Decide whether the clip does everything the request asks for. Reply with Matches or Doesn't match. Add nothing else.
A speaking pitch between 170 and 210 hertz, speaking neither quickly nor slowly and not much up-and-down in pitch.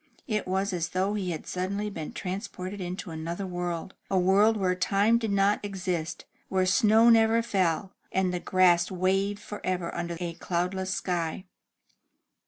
Matches